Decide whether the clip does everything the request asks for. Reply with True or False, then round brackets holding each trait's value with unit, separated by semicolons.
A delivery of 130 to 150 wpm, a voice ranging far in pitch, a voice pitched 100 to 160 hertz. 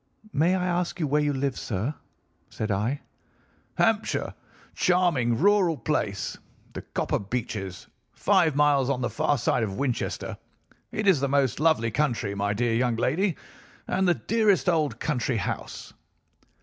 True (145 wpm; 6.7 semitones; 140 Hz)